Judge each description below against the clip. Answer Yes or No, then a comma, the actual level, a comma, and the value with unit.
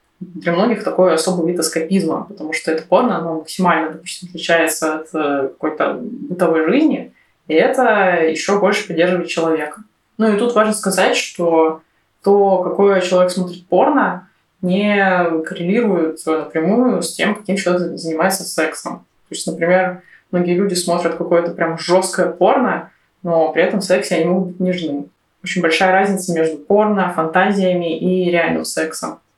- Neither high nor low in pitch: Yes, medium, 175 Hz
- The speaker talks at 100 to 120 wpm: No, average, 145 wpm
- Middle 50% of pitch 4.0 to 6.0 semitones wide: No, average, 2.7 semitones